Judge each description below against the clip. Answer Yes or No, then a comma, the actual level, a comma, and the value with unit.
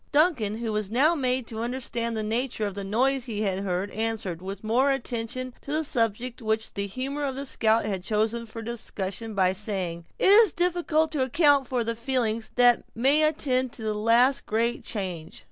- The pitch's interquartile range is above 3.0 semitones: Yes, average, 3.7 semitones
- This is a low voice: No, high, 230 Hz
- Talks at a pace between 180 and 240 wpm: Yes, average, 190 wpm